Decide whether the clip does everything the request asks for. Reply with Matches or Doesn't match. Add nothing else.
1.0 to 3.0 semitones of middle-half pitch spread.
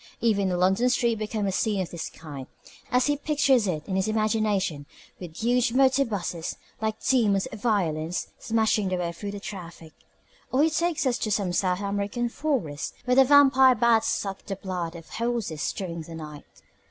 Doesn't match